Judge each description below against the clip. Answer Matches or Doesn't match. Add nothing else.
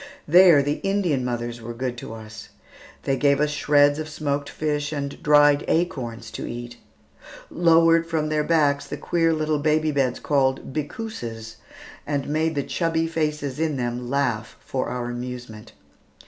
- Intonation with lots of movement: Doesn't match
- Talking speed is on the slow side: Doesn't match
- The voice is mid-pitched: Matches